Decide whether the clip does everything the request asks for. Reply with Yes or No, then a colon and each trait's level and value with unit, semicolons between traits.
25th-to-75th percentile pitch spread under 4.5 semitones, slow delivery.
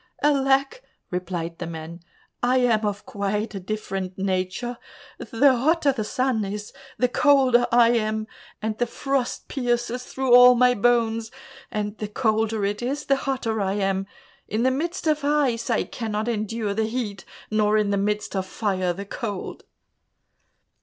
No: average, 3.6 semitones; average, 155 wpm